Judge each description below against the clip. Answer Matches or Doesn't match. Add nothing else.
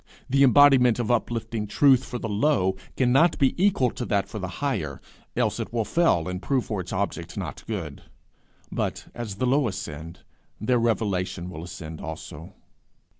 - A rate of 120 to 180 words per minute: Matches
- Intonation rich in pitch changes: Matches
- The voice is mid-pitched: Doesn't match